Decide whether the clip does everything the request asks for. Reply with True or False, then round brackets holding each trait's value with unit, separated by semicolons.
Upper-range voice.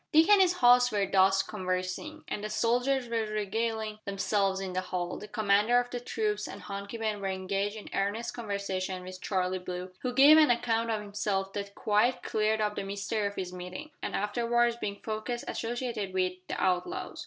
True (210 Hz)